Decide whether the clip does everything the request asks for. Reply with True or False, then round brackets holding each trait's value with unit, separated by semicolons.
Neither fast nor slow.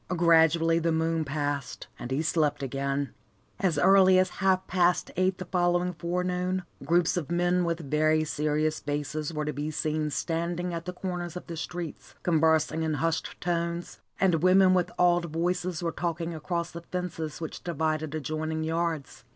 True (165 wpm)